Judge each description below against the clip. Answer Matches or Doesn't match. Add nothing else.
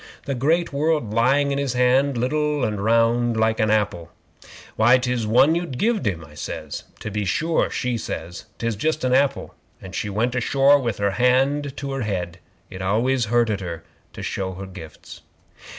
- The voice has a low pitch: Matches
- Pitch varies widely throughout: Doesn't match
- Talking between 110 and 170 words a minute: Doesn't match